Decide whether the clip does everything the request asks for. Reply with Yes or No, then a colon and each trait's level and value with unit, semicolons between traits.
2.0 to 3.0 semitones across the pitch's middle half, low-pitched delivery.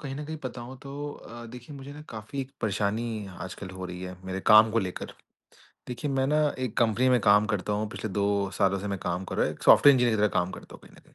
No: average, 4.2 semitones; low, 110 Hz